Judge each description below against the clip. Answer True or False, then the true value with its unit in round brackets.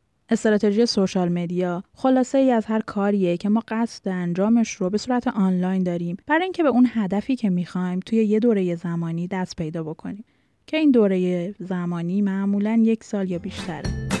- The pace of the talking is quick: True (170 wpm)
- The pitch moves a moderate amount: True (3.9 semitones)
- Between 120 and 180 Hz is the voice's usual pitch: False (200 Hz)